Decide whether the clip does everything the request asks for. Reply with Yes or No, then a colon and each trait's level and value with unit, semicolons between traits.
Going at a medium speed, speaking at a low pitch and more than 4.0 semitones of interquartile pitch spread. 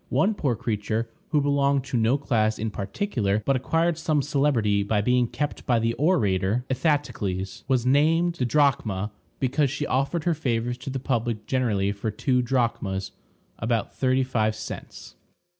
Yes: average, 155 wpm; low, 125 Hz; average, 4.6 semitones